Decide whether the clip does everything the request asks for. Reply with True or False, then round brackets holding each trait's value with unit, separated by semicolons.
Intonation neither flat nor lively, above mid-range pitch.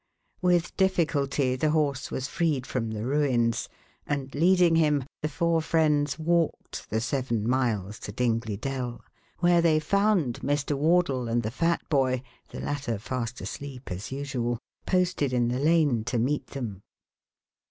False (4.7 semitones; 140 Hz)